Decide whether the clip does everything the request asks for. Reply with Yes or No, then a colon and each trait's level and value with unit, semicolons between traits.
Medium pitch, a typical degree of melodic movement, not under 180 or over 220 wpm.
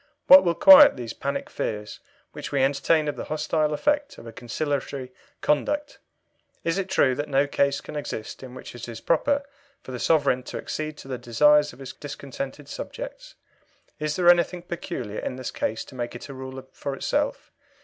Yes: medium, 145 Hz; average, 4.4 semitones; average, 190 wpm